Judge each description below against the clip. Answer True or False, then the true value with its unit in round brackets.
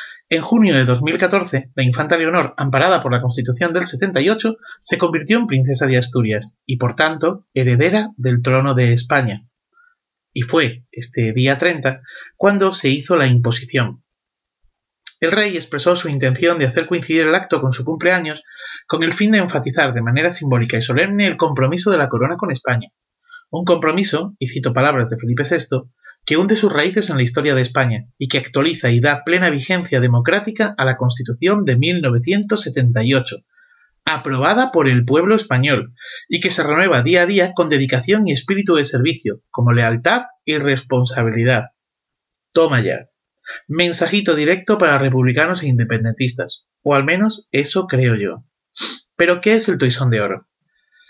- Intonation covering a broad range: True (5.7 semitones)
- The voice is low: False (145 Hz)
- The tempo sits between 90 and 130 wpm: False (165 wpm)